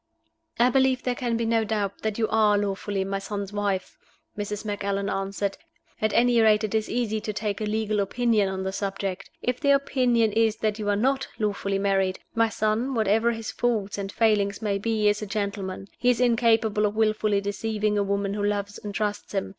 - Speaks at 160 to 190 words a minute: No, average, 200 wpm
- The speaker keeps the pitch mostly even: Yes, narrow, 2.0 semitones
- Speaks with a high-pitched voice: Yes, high, 210 Hz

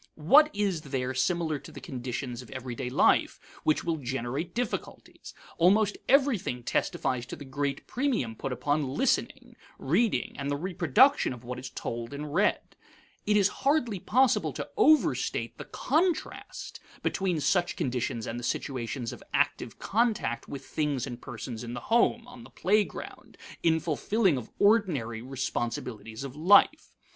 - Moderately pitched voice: Yes, medium, 145 Hz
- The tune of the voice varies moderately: No, wide, 8.6 semitones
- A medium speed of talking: Yes, average, 150 wpm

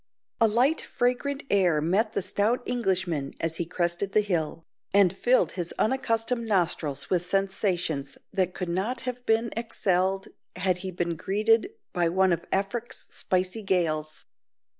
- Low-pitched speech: No, high, 190 Hz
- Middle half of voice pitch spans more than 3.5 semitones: Yes, average, 4.5 semitones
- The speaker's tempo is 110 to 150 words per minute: Yes, average, 145 wpm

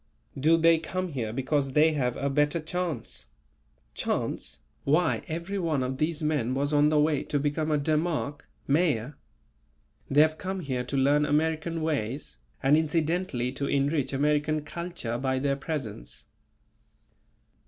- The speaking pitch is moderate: Yes, medium, 150 Hz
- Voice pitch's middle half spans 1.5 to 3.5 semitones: Yes, average, 2.8 semitones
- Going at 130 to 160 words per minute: Yes, average, 145 wpm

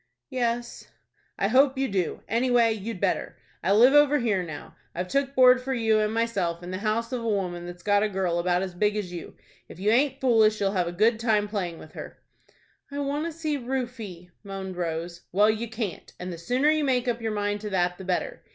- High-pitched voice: Yes, high, 215 Hz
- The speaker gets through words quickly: Yes, fast, 225 wpm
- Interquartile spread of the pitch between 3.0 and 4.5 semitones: No, average, 5.2 semitones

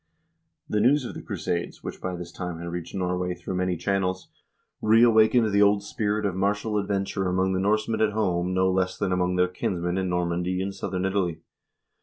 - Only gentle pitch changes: Yes, narrow, 2.3 semitones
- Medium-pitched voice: No, very low, 95 Hz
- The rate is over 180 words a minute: Yes, average, 200 wpm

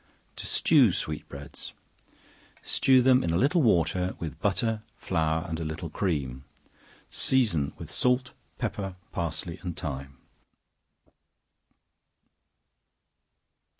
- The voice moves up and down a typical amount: No, wide, 5.9 semitones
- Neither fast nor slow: No, slow, 105 wpm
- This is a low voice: Yes, very low, 85 Hz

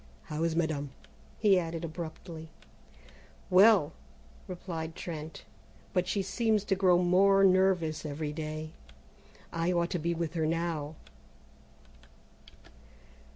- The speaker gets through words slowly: Yes, slow, 110 wpm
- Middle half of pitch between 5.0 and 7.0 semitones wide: No, average, 2.7 semitones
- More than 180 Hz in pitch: No, medium, 170 Hz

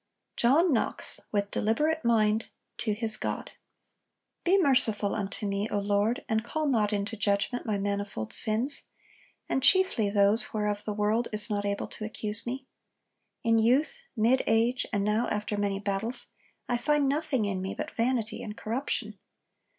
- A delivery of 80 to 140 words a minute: No, average, 160 wpm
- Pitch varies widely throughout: No, average, 3.2 semitones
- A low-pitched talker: No, high, 220 Hz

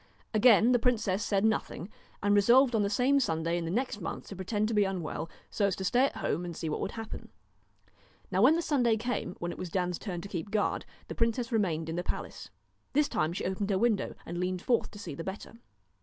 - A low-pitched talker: No, high, 205 Hz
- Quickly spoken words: Yes, fast, 235 wpm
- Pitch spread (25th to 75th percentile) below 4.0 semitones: No, average, 4.5 semitones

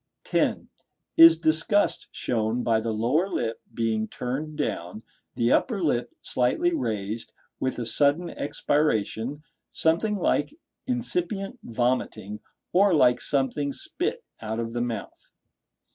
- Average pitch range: No, wide, 6.4 semitones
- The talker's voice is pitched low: Yes, low, 130 Hz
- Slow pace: Yes, slow, 120 wpm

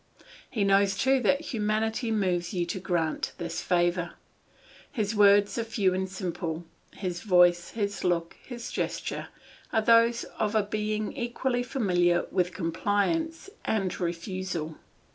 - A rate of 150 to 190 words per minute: No, slow, 135 wpm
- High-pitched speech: Yes, high, 200 Hz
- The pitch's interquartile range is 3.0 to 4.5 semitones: Yes, average, 4.0 semitones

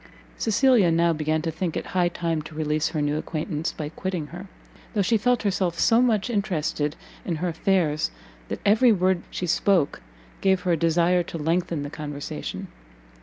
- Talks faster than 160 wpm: Yes, average, 175 wpm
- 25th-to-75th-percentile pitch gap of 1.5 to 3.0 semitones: No, average, 3.6 semitones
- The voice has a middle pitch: Yes, medium, 170 Hz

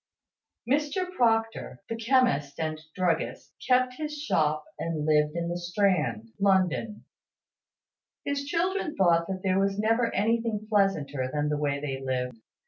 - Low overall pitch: No, high, 190 Hz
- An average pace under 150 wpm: Yes, slow, 135 wpm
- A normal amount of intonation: No, wide, 7.3 semitones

